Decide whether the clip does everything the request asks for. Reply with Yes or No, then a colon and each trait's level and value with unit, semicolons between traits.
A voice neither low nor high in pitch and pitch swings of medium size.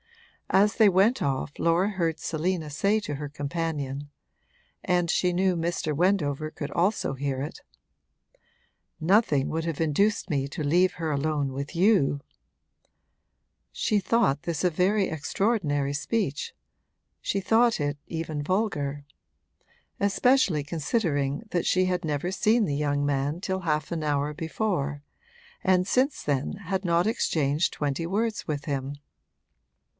Yes: medium, 165 Hz; average, 4.8 semitones